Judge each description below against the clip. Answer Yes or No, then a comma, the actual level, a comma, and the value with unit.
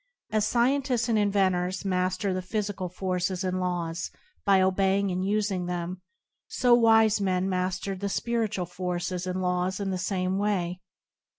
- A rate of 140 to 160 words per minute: Yes, average, 155 wpm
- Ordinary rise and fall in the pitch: No, narrow, 2.0 semitones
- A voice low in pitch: No, medium, 185 Hz